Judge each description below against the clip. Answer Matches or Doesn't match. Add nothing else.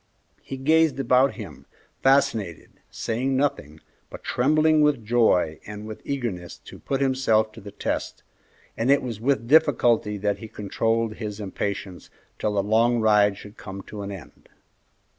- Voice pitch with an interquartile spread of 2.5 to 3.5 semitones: Doesn't match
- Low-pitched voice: Matches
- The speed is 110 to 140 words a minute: Doesn't match